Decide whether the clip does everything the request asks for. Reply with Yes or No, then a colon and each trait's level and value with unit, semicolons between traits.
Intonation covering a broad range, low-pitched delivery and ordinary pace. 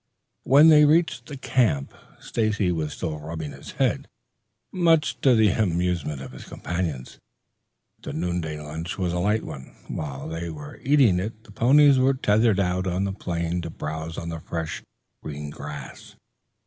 Yes: wide, 5.9 semitones; very low, 90 Hz; average, 160 wpm